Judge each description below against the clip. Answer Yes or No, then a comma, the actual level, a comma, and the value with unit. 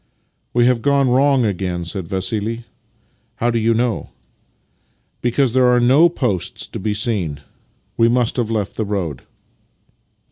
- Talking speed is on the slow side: No, average, 170 wpm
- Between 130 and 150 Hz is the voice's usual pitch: No, low, 115 Hz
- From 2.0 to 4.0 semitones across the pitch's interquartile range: Yes, average, 3.5 semitones